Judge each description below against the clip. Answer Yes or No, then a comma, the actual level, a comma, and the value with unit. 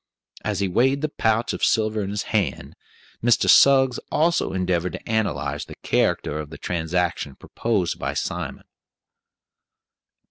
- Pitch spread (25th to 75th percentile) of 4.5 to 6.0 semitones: Yes, average, 5.0 semitones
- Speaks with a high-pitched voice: No, low, 100 Hz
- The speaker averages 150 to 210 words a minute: No, average, 140 wpm